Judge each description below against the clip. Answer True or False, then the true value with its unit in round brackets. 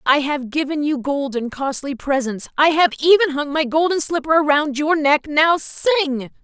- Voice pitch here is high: True (295 Hz)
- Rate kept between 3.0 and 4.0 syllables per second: False (5.0 syllables/s)